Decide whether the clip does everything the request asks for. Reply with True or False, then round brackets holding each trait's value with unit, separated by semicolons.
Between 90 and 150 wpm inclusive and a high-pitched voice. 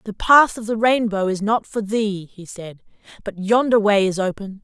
False (205 wpm; 210 Hz)